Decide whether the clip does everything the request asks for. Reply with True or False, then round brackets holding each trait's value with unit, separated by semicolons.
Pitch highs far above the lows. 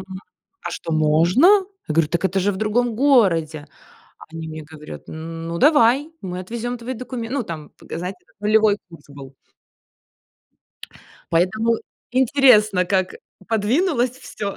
True (6.6 semitones)